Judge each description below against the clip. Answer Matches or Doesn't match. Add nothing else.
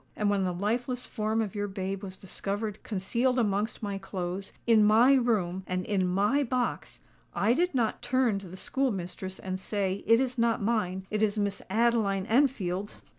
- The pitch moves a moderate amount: Matches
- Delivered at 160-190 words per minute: Matches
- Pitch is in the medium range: Doesn't match